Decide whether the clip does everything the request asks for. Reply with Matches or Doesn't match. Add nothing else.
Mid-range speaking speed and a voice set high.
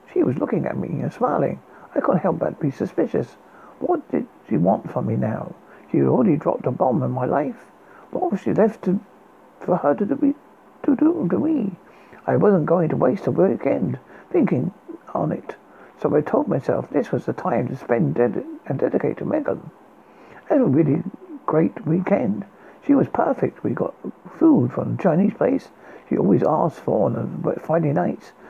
Matches